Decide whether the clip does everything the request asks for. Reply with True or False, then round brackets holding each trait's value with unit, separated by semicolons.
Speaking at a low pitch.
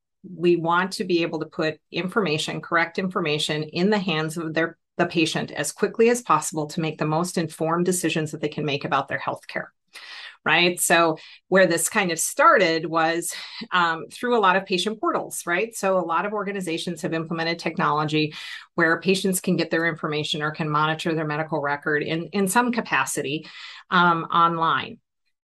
False (165 Hz)